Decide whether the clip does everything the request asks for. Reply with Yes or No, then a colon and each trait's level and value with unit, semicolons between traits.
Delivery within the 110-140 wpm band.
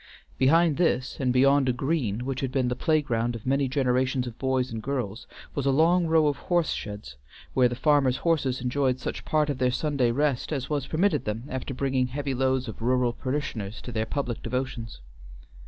No: average, 195 wpm